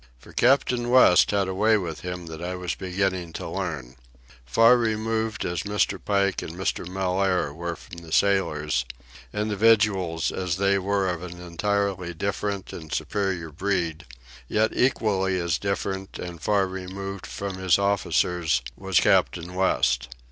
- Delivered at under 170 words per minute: Yes, average, 150 wpm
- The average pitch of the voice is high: No, very low, 95 Hz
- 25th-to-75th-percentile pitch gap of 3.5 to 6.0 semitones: No, narrow, 2.6 semitones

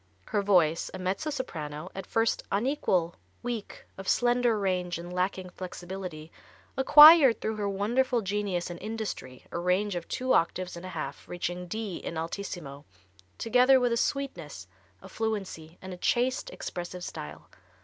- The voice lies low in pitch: No, high, 190 Hz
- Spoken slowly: No, average, 150 wpm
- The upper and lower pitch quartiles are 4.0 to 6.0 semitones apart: Yes, average, 4.6 semitones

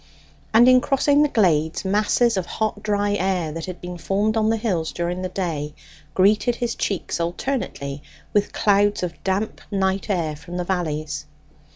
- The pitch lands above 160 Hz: Yes, high, 190 Hz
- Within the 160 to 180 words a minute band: Yes, average, 170 wpm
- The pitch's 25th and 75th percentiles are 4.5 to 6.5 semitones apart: No, average, 4.0 semitones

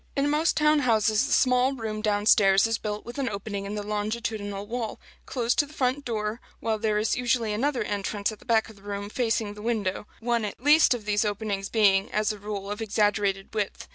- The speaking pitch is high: Yes, high, 215 Hz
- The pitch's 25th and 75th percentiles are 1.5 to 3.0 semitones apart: Yes, narrow, 2.6 semitones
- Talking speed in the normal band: No, fast, 220 wpm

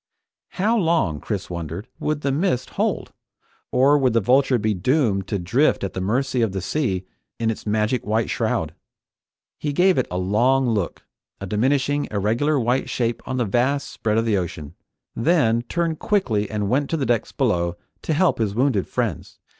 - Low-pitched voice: Yes, low, 120 Hz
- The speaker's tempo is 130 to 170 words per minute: No, average, 180 wpm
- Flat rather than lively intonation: No, wide, 5.4 semitones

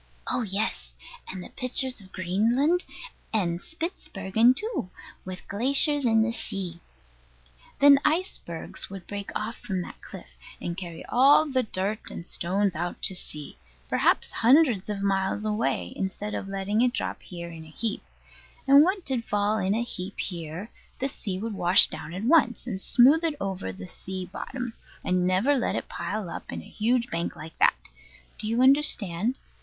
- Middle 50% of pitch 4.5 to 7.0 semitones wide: Yes, average, 5.3 semitones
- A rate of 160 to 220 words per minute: Yes, average, 170 wpm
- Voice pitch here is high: Yes, high, 205 Hz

